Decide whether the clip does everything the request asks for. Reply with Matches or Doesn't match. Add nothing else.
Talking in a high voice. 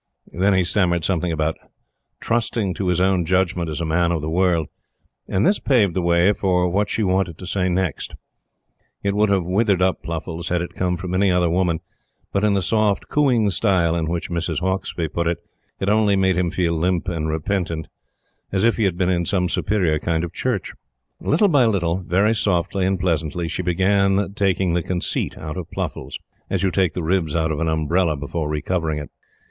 Doesn't match